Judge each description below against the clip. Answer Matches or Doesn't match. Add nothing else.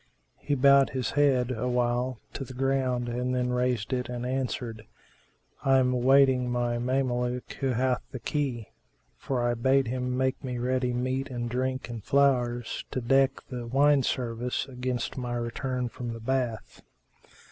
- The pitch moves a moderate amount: Doesn't match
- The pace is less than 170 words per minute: Matches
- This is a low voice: Matches